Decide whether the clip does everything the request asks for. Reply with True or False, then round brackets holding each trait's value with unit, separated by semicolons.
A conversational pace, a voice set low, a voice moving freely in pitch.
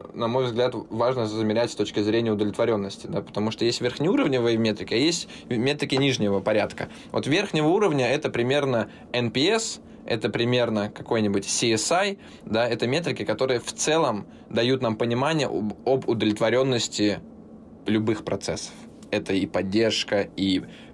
False (135 wpm; 115 Hz; 2.8 semitones)